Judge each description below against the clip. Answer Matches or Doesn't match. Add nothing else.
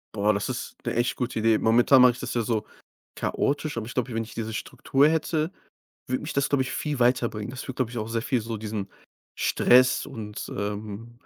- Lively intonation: Doesn't match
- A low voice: Matches